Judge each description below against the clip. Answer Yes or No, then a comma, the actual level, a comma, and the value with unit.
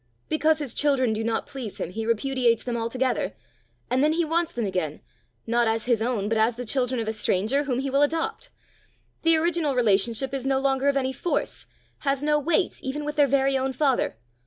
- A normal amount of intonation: Yes, average, 3.9 semitones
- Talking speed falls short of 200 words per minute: No, fast, 205 wpm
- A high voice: Yes, very high, 265 Hz